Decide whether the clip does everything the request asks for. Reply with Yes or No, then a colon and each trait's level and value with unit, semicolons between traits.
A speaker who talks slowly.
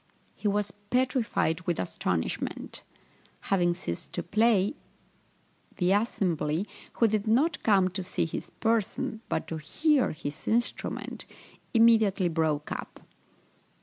Yes: slow, 115 wpm